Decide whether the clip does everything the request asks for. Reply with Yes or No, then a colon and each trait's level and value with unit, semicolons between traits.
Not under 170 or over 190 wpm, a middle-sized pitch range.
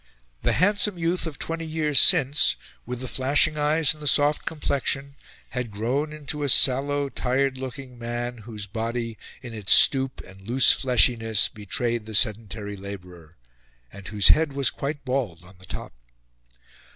No: average, 160 wpm; average, 4.7 semitones